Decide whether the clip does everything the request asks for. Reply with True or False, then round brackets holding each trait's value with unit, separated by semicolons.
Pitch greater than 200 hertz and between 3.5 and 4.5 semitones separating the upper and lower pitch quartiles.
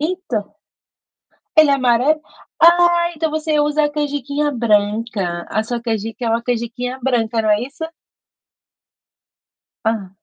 False (250 Hz; 5.1 semitones)